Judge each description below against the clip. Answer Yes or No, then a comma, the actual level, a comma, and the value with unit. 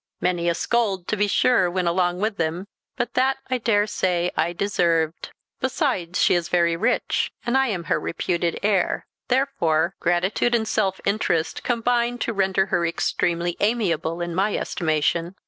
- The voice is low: No, medium, 185 Hz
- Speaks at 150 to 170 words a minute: Yes, average, 160 wpm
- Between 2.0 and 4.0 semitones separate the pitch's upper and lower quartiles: No, average, 4.4 semitones